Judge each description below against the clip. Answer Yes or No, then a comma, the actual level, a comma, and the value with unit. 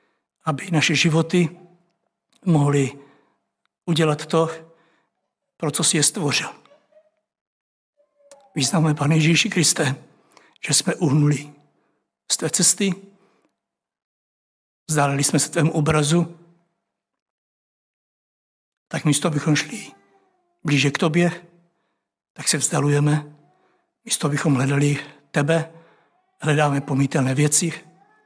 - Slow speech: Yes, slow, 90 wpm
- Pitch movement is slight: No, average, 3.3 semitones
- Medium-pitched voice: Yes, medium, 160 Hz